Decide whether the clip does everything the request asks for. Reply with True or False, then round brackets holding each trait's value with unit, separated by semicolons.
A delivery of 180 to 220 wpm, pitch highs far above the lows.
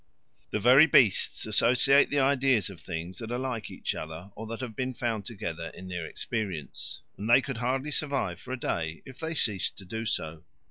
True (200 wpm; 5.9 semitones)